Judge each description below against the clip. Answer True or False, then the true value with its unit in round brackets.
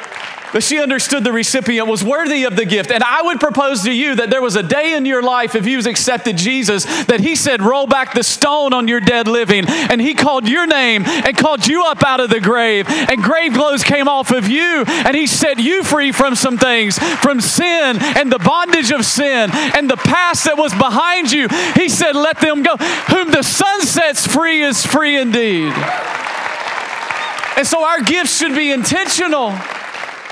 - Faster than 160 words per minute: True (200 wpm)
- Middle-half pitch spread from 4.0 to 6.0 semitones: True (4.3 semitones)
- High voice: True (275 Hz)